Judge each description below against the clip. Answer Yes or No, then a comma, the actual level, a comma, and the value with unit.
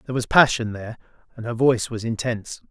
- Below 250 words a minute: Yes, average, 200 wpm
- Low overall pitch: Yes, low, 115 Hz